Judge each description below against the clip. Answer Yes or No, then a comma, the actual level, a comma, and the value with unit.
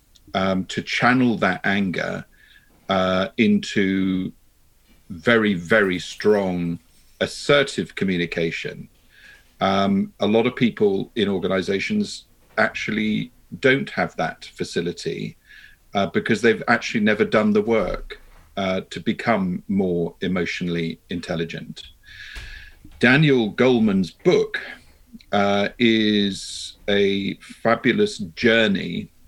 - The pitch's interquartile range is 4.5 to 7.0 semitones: Yes, average, 5.1 semitones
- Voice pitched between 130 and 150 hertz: No, low, 100 Hz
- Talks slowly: Yes, slow, 95 wpm